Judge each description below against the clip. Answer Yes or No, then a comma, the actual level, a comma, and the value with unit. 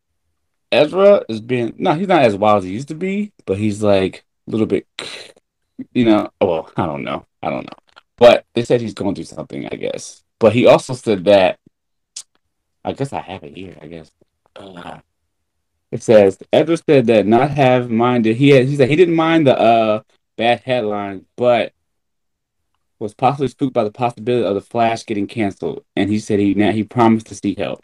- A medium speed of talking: Yes, average, 195 wpm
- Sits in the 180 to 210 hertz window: No, low, 110 Hz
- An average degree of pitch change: Yes, average, 4.3 semitones